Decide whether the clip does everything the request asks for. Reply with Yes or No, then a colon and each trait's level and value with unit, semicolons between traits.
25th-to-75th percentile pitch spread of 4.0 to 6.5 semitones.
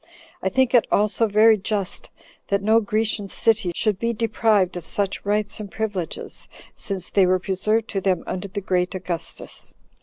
No: average, 2.8 semitones